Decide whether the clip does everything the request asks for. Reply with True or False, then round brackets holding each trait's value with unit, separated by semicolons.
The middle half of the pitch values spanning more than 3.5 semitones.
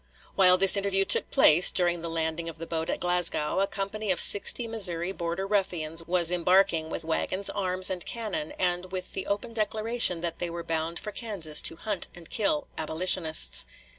False (2.9 semitones)